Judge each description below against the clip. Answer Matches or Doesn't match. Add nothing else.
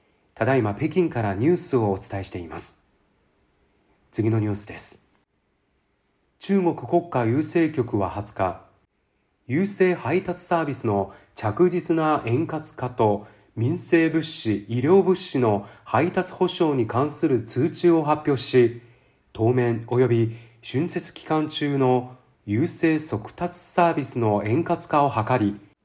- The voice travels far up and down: Matches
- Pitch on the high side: Doesn't match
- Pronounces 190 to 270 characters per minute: Matches